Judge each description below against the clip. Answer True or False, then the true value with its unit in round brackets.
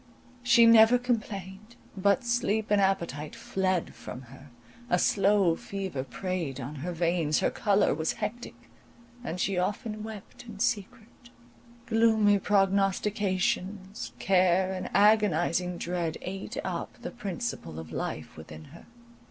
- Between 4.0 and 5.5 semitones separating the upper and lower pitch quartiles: False (3.6 semitones)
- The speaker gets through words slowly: True (125 wpm)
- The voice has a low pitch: False (195 Hz)